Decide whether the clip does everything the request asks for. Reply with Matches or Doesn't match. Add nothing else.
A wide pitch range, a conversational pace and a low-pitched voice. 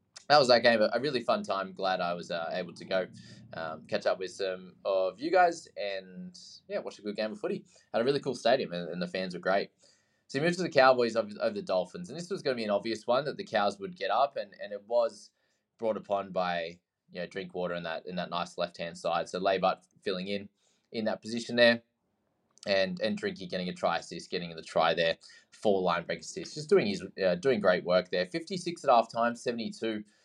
Doesn't match